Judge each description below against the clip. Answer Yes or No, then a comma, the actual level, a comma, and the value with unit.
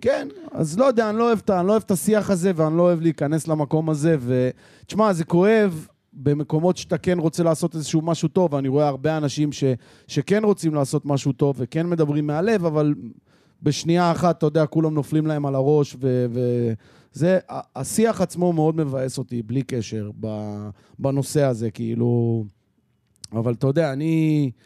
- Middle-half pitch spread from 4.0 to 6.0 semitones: Yes, average, 4.3 semitones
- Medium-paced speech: No, fast, 180 wpm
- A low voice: No, medium, 155 Hz